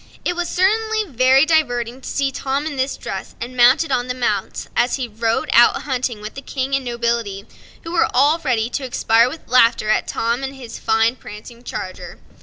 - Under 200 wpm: No, fast, 205 wpm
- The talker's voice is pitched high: Yes, very high, 255 Hz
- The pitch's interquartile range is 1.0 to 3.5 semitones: Yes, average, 2.9 semitones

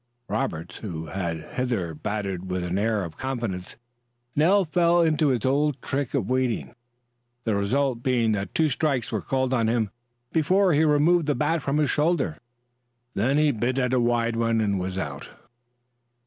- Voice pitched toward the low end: Yes, low, 125 Hz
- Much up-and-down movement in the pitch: Yes, wide, 6.6 semitones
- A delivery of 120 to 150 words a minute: No, average, 170 wpm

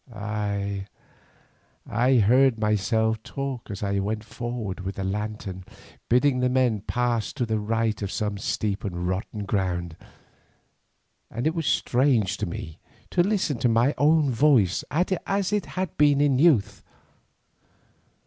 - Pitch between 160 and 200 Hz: No, low, 110 Hz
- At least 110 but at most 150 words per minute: Yes, average, 140 wpm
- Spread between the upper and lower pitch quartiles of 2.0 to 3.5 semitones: No, average, 4.8 semitones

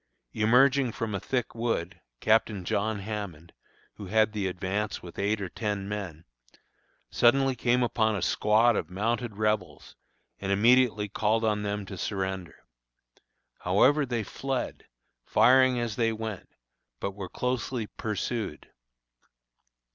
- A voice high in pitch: No, low, 110 Hz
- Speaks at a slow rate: Yes, slow, 130 wpm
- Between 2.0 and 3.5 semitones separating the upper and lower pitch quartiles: Yes, average, 3.2 semitones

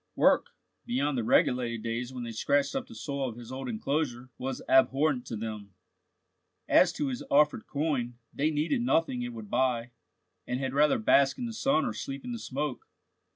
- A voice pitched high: No, low, 130 Hz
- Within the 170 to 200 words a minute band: Yes, average, 190 wpm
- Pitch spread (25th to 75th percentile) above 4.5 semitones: No, average, 3.8 semitones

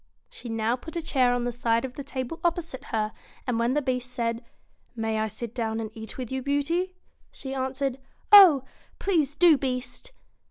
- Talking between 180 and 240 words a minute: Yes, average, 200 wpm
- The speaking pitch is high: Yes, very high, 255 Hz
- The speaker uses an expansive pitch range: No, average, 3.6 semitones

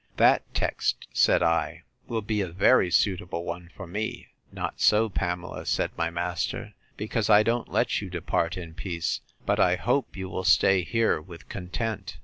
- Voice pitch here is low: Yes, very low, 95 Hz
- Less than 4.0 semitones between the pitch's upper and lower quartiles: Yes, average, 3.6 semitones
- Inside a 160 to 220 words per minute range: Yes, average, 170 wpm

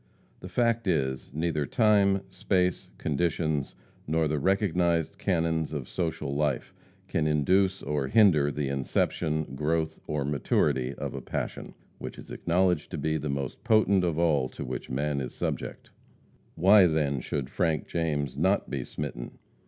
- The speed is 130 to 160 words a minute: Yes, average, 150 wpm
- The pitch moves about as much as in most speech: Yes, average, 4.0 semitones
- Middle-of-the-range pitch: No, very low, 80 Hz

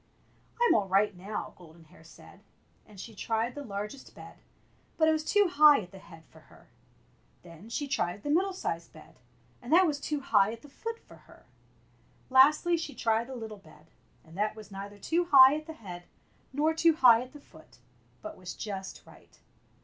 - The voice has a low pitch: No, high, 230 Hz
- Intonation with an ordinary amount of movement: No, wide, 7.5 semitones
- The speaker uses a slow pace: No, average, 195 wpm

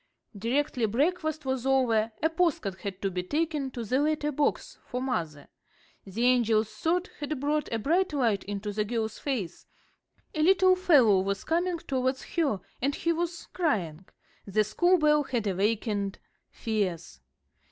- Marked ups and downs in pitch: Yes, wide, 6.7 semitones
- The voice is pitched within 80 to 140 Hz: No, very high, 255 Hz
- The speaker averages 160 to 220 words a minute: No, average, 150 wpm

